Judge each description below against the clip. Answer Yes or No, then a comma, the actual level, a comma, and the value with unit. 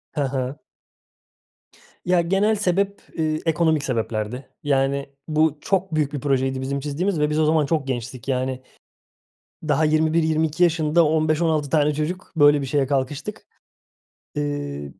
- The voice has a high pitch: No, medium, 150 Hz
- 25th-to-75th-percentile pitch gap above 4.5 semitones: No, average, 2.8 semitones